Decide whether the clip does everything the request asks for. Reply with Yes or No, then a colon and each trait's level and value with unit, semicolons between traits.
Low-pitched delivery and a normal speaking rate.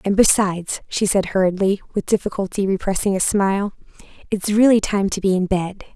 No: high, 195 Hz; average, 170 wpm